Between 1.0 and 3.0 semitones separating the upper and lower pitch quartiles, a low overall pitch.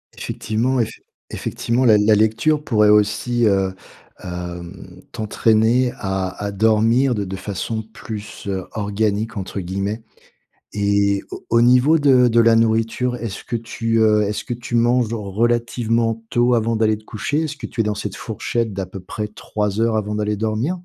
Yes: narrow, 2.4 semitones; low, 110 Hz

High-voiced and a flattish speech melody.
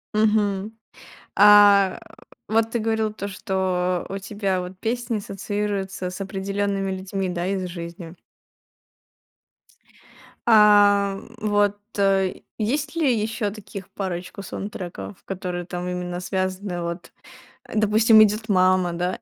Yes: high, 195 Hz; narrow, 2.3 semitones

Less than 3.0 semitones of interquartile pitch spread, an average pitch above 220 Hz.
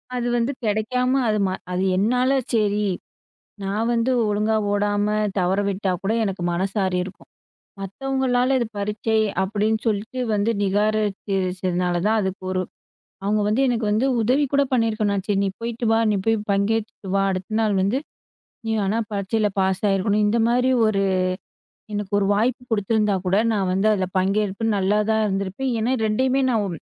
No: narrow, 2.5 semitones; high, 210 Hz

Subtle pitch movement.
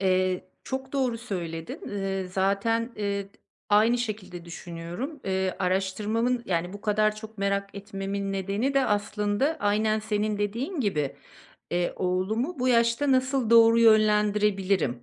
No: average, 3.2 semitones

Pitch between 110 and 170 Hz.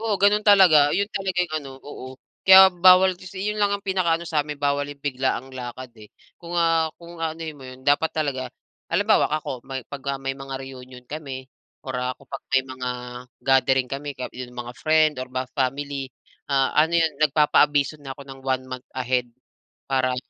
Yes: medium, 140 Hz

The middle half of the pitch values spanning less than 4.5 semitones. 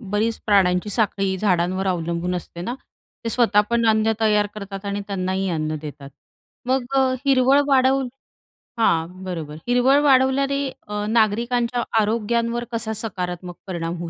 No: average, 4.8 semitones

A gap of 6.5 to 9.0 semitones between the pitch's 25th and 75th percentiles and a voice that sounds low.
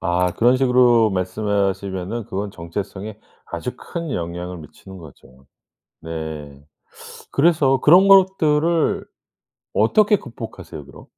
Yes: wide, 7.4 semitones; low, 100 Hz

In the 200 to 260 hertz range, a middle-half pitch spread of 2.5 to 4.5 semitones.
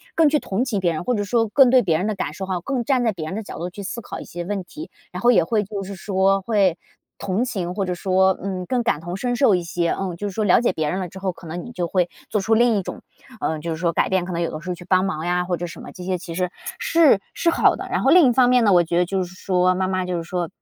No: high, 190 Hz; average, 3.6 semitones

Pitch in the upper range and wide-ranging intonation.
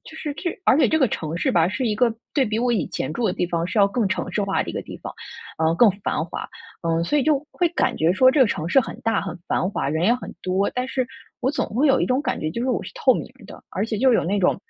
Yes: high, 225 Hz; wide, 6.3 semitones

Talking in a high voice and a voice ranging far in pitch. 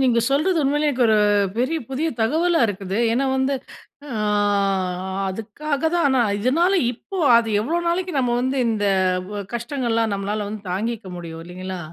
Yes: high, 245 Hz; wide, 5.8 semitones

